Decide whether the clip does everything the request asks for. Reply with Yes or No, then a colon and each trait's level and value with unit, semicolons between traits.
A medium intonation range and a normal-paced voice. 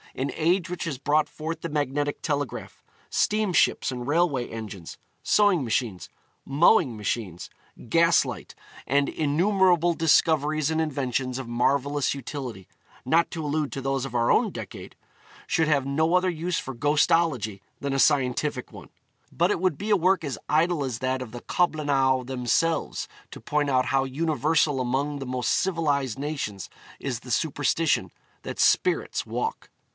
Yes: average, 4.1 semitones; average, 155 wpm